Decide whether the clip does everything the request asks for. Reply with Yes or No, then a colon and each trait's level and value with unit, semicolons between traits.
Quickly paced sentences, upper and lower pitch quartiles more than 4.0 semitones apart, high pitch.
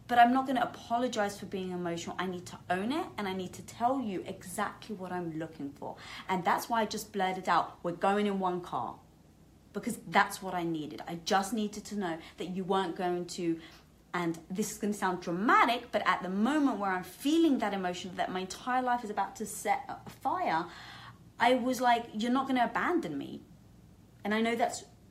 Yes: fast, 215 wpm; average, 4.5 semitones; high, 200 Hz